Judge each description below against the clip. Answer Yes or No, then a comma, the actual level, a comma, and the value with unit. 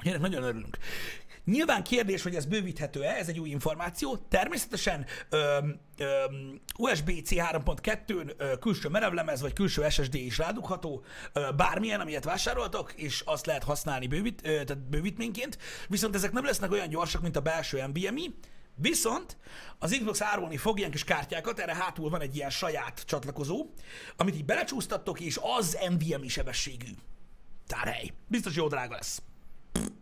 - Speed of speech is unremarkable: Yes, average, 140 wpm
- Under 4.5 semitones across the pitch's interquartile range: No, wide, 5.9 semitones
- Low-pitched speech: No, medium, 165 Hz